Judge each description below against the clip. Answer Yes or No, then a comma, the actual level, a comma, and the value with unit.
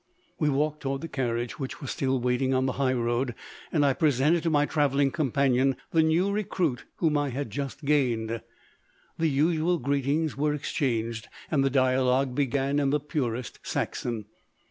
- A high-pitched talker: No, medium, 140 Hz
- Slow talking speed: No, average, 165 wpm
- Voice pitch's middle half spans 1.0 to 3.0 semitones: Yes, average, 2.7 semitones